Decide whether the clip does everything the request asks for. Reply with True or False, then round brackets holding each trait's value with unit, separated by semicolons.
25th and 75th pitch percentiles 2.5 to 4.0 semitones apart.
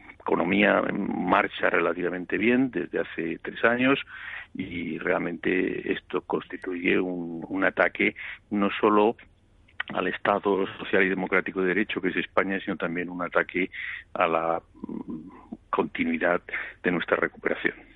False (4.5 semitones)